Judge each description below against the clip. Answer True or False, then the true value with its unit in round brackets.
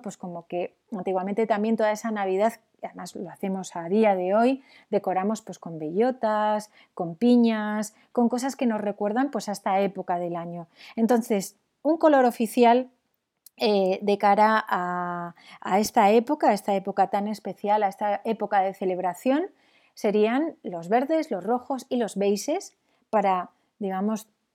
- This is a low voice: False (215 Hz)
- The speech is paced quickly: False (155 wpm)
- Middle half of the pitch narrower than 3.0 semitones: False (3.6 semitones)